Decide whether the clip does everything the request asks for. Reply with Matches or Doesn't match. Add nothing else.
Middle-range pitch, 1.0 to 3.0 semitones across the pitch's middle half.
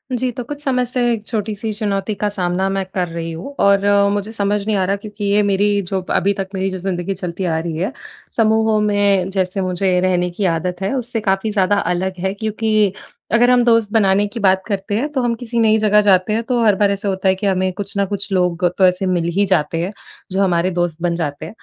Doesn't match